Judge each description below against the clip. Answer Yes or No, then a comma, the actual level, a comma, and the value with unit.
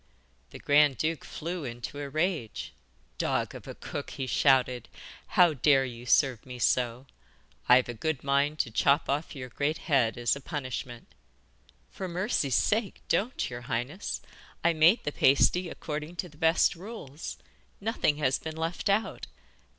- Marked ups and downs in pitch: No, average, 4.4 semitones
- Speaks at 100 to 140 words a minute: No, average, 160 wpm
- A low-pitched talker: No, medium, 145 Hz